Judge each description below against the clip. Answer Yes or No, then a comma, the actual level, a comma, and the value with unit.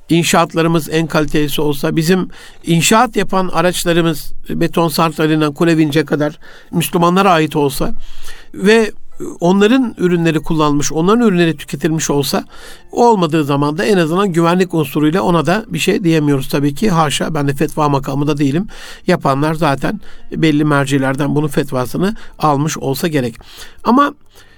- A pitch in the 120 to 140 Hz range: No, medium, 165 Hz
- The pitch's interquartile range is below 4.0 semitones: Yes, average, 3.1 semitones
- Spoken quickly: No, average, 130 wpm